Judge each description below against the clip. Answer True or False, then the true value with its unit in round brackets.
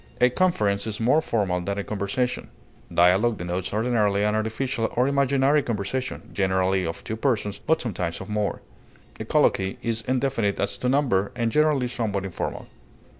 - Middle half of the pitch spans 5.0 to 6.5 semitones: False (4.3 semitones)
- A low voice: True (110 Hz)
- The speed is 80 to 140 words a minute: False (160 wpm)